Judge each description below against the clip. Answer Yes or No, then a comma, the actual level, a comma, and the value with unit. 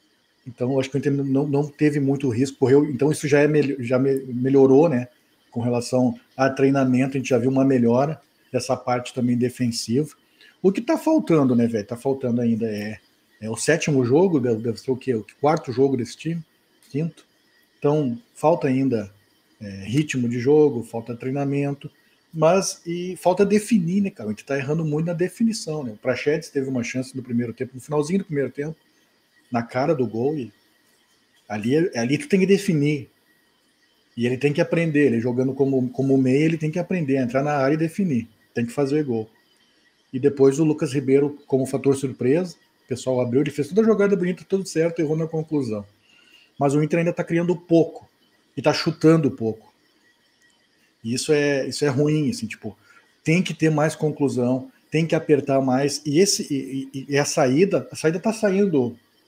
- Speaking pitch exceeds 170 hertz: No, medium, 140 Hz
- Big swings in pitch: No, average, 3.7 semitones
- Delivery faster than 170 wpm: Yes, fast, 185 wpm